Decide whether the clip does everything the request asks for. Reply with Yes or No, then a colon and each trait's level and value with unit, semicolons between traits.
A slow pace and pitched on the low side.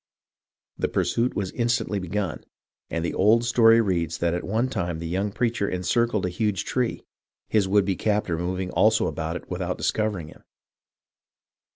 No: average, 165 wpm; low, 100 Hz